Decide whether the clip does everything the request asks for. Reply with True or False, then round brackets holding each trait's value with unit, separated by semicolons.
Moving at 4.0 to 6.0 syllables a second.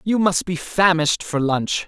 True (4.5 syllables/s)